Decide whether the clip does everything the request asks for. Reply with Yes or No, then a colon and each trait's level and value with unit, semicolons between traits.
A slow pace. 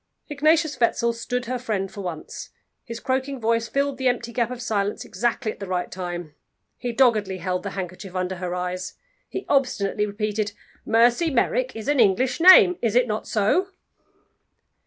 No: average, 170 wpm